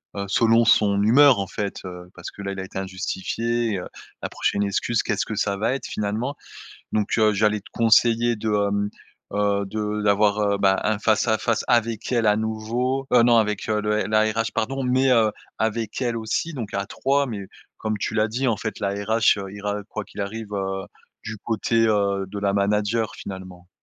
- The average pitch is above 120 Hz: No, low, 105 Hz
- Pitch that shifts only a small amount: Yes, narrow, 2.2 semitones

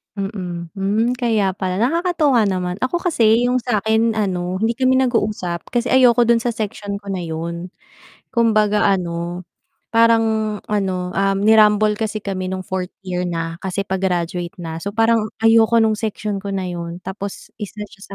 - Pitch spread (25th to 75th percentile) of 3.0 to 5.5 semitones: Yes, average, 3.6 semitones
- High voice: Yes, high, 205 Hz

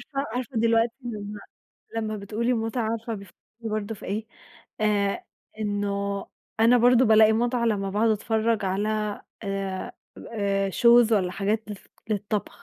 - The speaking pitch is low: No, high, 215 Hz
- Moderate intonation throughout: No, narrow, 2.1 semitones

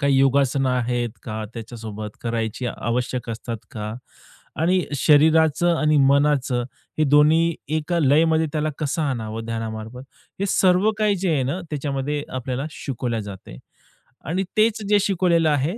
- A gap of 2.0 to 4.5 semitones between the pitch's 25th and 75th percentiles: No, average, 5.1 semitones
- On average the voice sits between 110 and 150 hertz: Yes, medium, 140 Hz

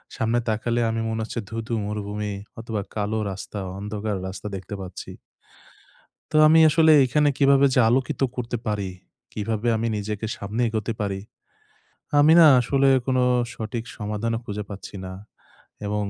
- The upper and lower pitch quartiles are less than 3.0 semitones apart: Yes, narrow, 2.6 semitones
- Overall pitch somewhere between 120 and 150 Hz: No, low, 110 Hz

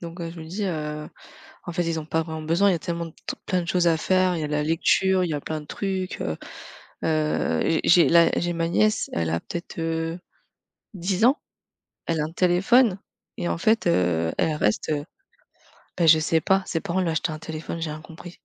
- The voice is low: No, medium, 165 Hz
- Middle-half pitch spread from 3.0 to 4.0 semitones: No, narrow, 2.5 semitones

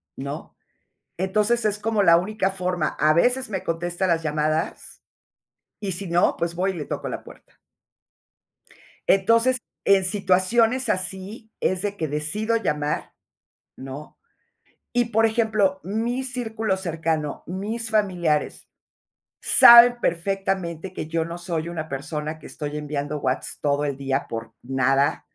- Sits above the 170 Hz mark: Yes, medium, 185 Hz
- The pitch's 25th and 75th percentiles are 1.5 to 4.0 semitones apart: No, wide, 5.5 semitones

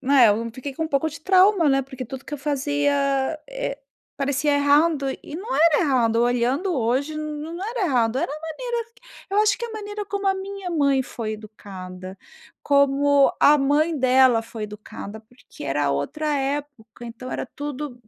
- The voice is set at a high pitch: Yes, very high, 280 Hz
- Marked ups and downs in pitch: No, average, 4.6 semitones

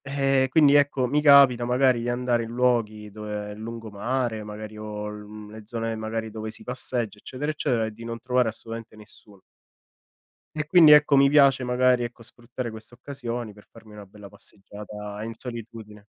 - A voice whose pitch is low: Yes, low, 115 Hz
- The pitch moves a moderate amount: Yes, average, 3.0 semitones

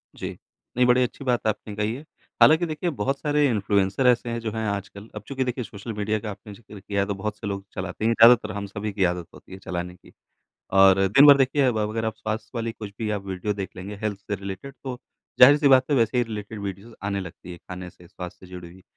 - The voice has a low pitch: Yes, low, 105 Hz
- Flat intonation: No, average, 3.7 semitones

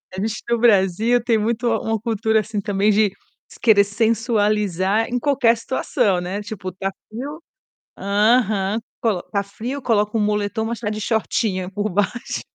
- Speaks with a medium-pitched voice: No, high, 215 Hz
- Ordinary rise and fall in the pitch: No, narrow, 2.3 semitones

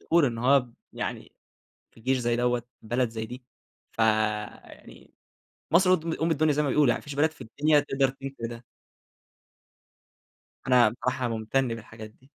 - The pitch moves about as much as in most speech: Yes, average, 3.8 semitones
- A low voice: Yes, low, 125 Hz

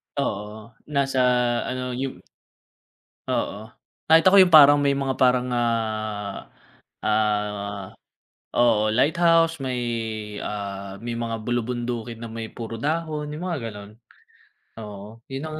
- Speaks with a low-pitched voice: Yes, low, 120 Hz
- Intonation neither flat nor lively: Yes, average, 4.6 semitones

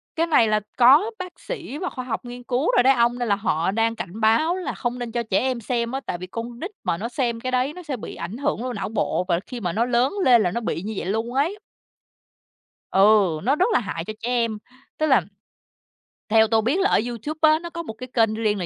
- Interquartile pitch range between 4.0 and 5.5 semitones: No, average, 3.5 semitones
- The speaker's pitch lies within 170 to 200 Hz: No, high, 240 Hz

